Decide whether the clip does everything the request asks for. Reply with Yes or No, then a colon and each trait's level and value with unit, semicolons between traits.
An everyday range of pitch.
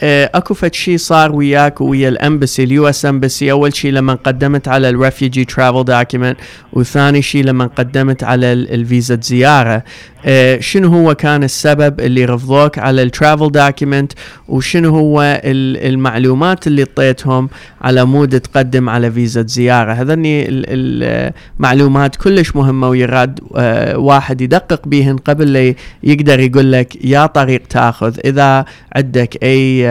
No: narrow, 2.2 semitones